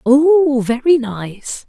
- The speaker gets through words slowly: Yes, slow, 105 wpm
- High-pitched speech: Yes, very high, 265 Hz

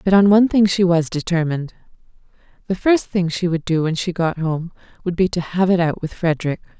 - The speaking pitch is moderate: Yes, medium, 175 Hz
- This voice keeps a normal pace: No, fast, 220 wpm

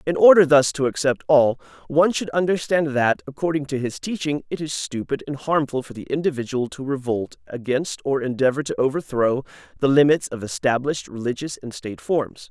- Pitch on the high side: No, low, 135 Hz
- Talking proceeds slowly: No, average, 180 wpm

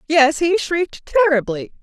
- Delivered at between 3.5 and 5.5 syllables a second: Yes, 5.0 syllables/s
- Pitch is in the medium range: No, very high, 315 Hz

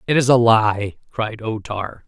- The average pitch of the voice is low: Yes, low, 110 Hz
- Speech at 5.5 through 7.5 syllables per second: No, 3.9 syllables/s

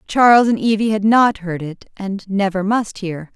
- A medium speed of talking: Yes, average, 195 wpm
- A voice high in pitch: Yes, high, 200 Hz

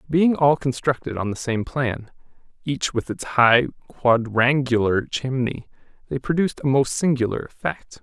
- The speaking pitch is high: No, low, 130 Hz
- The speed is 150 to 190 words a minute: No, average, 140 wpm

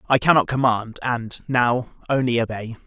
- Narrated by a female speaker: No, male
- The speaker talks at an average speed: Yes, average, 145 wpm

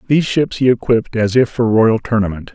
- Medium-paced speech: No, fast, 210 wpm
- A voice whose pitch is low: Yes, low, 115 Hz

